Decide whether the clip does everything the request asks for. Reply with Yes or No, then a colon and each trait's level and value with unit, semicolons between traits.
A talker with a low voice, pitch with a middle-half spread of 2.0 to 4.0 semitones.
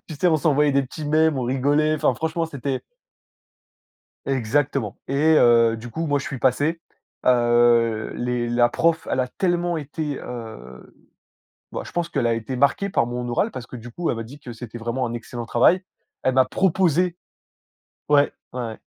No: low, 130 Hz; average, 4.5 semitones